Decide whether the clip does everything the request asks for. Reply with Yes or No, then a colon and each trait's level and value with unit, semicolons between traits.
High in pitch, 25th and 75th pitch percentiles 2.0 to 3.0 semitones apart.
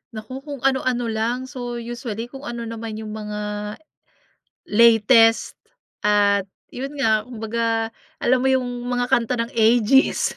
Yes: high, 230 Hz; narrow, 2.4 semitones